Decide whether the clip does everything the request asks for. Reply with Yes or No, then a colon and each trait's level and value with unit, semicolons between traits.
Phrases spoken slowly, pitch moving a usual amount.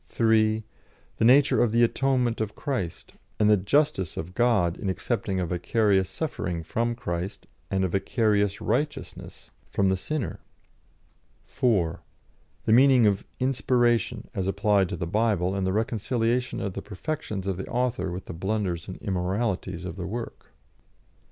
No: average, 150 wpm; average, 4.1 semitones